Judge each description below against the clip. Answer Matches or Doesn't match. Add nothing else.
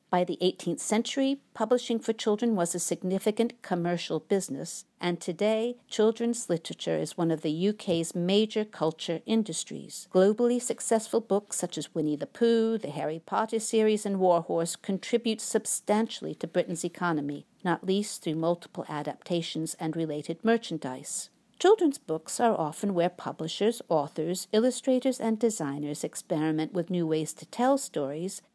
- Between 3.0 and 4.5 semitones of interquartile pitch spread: Doesn't match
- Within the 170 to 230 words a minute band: Doesn't match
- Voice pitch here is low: Doesn't match